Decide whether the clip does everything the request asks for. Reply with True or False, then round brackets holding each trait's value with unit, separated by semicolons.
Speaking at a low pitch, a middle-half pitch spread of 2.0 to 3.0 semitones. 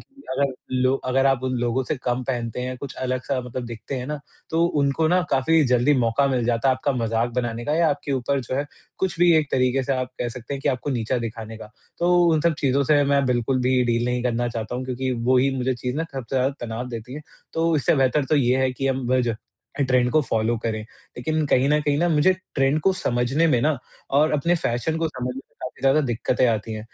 True (130 Hz; 2.7 semitones)